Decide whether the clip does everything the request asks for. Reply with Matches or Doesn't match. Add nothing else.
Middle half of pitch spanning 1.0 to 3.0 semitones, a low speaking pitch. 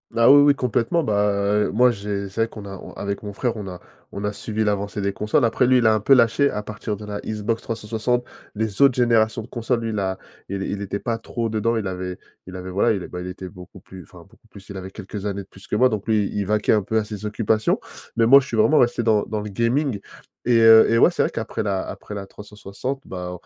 Matches